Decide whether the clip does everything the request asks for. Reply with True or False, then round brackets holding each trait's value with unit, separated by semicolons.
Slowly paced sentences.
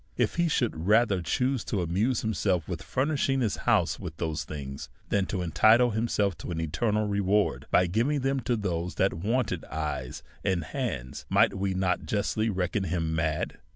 False (185 wpm)